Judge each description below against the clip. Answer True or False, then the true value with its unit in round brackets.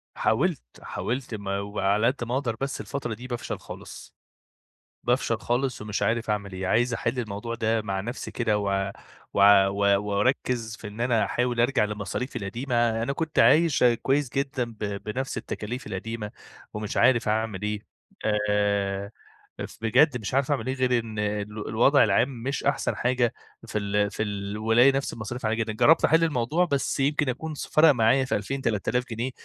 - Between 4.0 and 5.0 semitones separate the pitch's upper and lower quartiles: False (3.6 semitones)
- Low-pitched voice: True (115 Hz)